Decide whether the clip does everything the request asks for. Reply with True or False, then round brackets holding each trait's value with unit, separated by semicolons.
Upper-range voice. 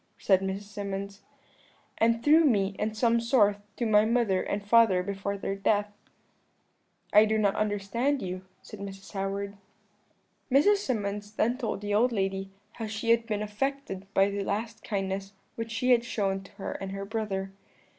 True (205 Hz)